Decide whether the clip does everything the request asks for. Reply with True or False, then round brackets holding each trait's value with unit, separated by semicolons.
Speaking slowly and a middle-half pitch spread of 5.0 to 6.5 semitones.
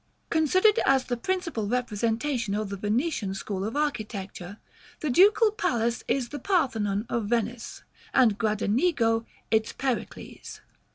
True (125 wpm; 5.4 semitones)